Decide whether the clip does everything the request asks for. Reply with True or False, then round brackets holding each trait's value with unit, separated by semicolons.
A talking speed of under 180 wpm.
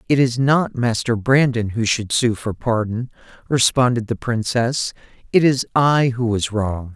True (165 wpm)